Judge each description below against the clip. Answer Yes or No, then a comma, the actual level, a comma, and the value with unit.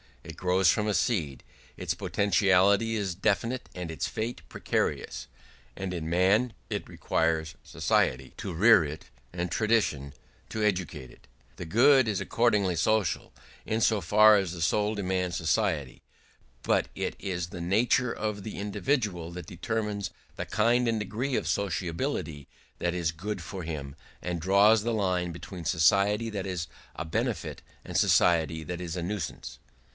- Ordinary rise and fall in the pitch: Yes, average, 4.2 semitones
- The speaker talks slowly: No, average, 155 wpm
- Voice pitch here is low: Yes, very low, 95 Hz